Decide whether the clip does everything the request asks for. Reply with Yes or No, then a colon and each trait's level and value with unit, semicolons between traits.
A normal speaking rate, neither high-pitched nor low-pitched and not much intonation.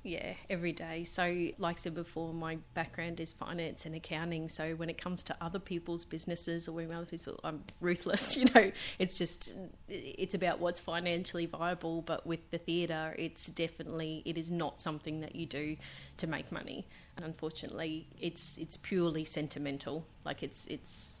Yes: average, 175 wpm; medium, 165 Hz; narrow, 1.3 semitones